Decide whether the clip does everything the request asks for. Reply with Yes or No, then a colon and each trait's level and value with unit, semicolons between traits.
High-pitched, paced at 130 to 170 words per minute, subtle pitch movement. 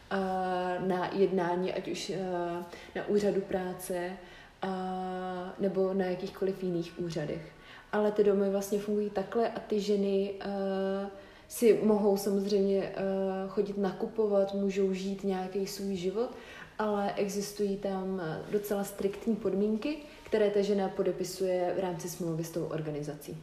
No: high, 195 Hz; average, 120 wpm; narrow, 1.6 semitones